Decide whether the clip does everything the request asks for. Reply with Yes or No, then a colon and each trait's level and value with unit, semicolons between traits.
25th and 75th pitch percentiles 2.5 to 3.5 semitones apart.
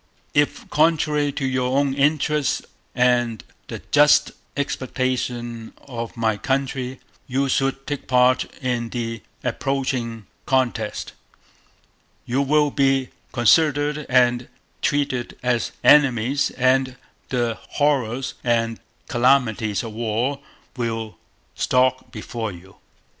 Yes: average, 2.8 semitones